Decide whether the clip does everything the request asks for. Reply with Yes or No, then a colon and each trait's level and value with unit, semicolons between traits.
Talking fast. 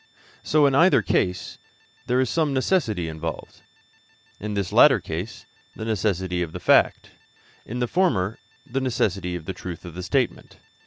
No: average, 150 wpm